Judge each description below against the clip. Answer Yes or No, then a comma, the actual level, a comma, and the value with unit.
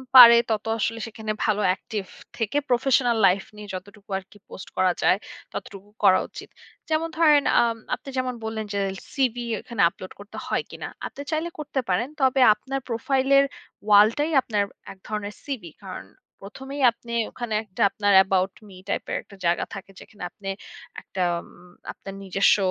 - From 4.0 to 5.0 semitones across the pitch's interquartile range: Yes, average, 4.6 semitones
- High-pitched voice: Yes, high, 215 Hz